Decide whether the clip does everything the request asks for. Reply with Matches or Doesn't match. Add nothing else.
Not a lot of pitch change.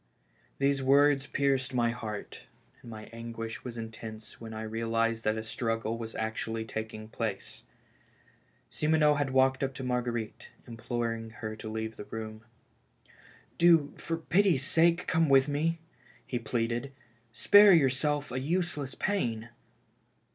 Doesn't match